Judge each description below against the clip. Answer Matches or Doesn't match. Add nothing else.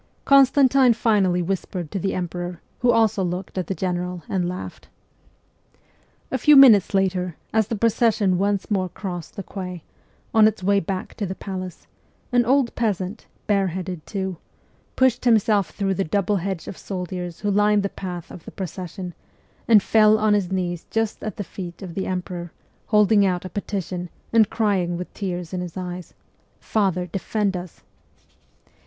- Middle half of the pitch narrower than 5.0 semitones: Matches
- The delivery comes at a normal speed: Matches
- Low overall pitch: Doesn't match